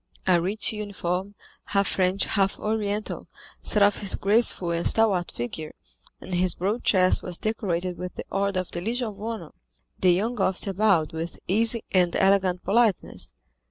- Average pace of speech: Yes, average, 160 wpm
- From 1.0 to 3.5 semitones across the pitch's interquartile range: Yes, average, 2.8 semitones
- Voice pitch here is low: No, high, 195 Hz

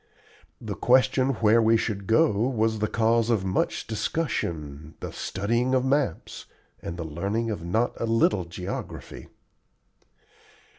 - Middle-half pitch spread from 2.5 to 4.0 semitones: Yes, average, 3.7 semitones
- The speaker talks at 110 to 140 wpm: Yes, slow, 135 wpm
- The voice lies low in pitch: Yes, low, 110 Hz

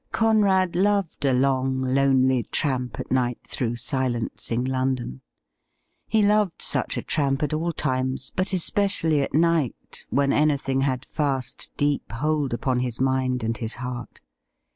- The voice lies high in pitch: No, low, 135 Hz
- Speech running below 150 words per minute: Yes, average, 140 wpm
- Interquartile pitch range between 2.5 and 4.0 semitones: Yes, average, 3.4 semitones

